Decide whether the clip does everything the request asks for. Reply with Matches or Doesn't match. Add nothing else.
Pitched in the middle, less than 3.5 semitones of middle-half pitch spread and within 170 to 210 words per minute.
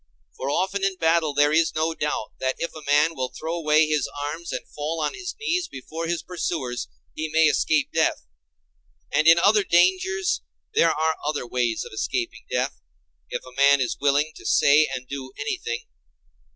Matches